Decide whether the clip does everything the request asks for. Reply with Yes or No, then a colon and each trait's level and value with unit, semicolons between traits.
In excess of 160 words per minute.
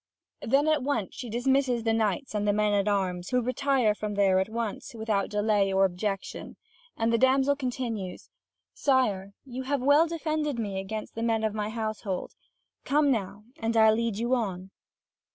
Yes: average, 175 wpm